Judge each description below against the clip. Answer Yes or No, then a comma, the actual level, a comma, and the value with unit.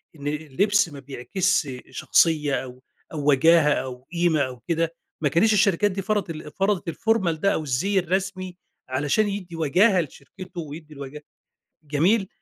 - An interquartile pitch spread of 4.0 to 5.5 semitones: Yes, average, 4.8 semitones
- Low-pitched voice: No, medium, 165 Hz